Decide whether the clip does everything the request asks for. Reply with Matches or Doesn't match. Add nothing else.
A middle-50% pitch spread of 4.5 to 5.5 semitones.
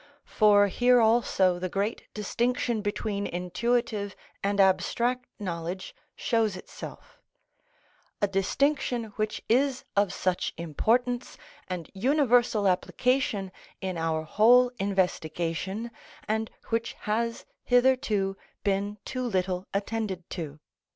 Doesn't match